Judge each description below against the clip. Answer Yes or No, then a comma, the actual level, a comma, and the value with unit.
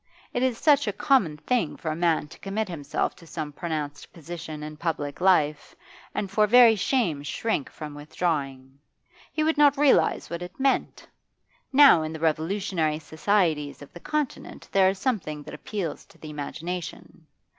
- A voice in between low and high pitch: Yes, medium, 170 Hz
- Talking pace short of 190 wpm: Yes, average, 165 wpm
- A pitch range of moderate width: No, wide, 5.8 semitones